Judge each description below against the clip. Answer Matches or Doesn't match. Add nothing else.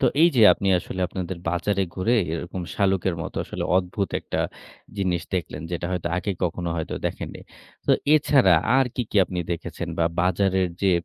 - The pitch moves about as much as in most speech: Doesn't match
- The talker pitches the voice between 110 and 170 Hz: Doesn't match